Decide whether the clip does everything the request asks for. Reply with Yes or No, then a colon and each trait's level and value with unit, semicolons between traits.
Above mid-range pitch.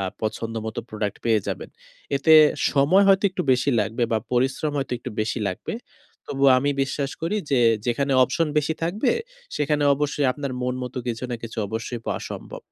No: low, 135 Hz